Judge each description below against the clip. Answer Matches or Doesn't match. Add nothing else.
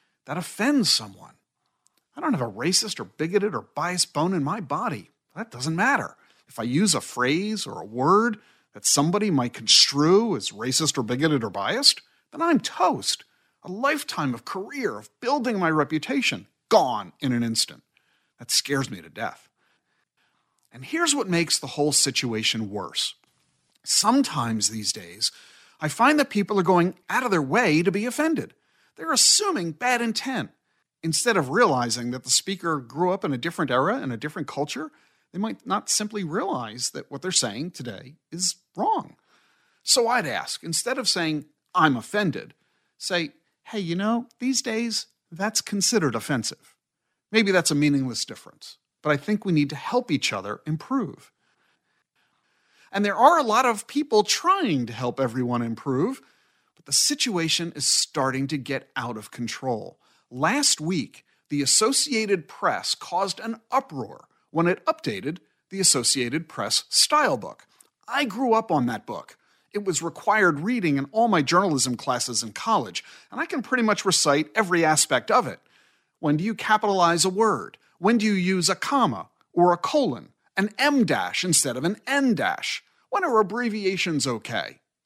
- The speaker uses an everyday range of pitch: Doesn't match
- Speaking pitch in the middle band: Matches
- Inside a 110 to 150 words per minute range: Doesn't match